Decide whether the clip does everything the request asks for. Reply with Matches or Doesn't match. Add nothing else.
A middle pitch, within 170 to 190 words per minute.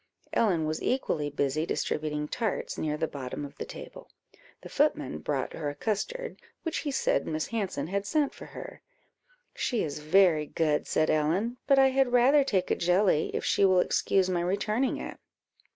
Matches